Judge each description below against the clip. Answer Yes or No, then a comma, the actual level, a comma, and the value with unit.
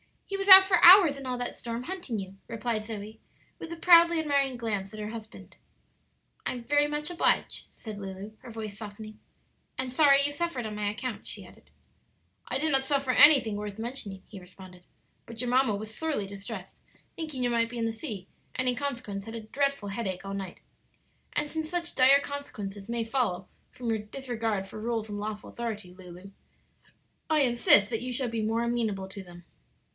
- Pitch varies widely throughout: No, average, 5.0 semitones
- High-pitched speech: Yes, high, 230 Hz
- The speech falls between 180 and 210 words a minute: Yes, average, 190 wpm